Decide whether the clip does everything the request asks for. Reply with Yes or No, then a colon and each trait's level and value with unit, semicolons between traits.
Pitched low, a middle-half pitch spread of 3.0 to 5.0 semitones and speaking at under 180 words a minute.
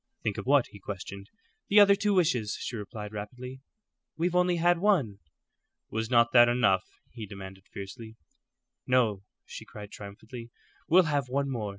No: low, 120 Hz; wide, 5.6 semitones; average, 160 wpm